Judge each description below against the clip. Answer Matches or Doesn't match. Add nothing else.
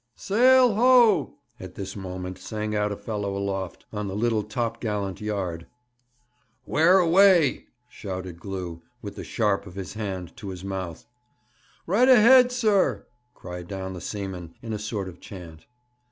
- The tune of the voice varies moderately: Doesn't match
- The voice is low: Matches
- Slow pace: Doesn't match